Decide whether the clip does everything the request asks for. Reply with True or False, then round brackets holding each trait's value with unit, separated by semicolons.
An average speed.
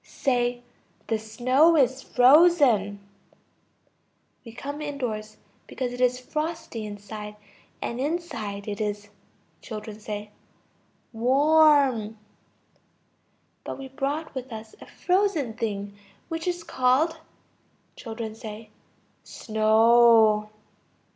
False (90 wpm)